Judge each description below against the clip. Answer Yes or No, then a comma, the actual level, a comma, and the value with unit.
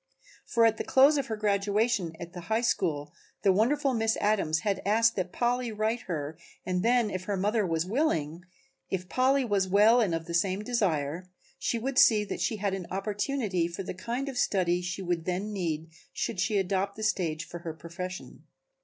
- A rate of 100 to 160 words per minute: No, average, 200 wpm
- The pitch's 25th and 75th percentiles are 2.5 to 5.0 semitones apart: Yes, average, 4.2 semitones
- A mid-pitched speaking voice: No, high, 200 Hz